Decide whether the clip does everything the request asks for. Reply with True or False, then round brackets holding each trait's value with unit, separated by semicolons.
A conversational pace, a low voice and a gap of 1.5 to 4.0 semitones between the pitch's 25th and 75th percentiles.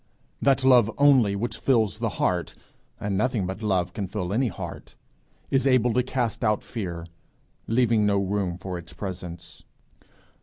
False (155 wpm; 105 Hz; 4.7 semitones)